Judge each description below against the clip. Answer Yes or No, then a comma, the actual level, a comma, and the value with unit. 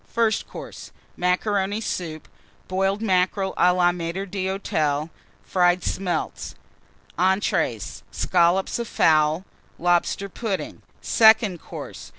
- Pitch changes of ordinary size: No, narrow, 2.1 semitones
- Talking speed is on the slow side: Yes, slow, 100 wpm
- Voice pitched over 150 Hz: Yes, medium, 185 Hz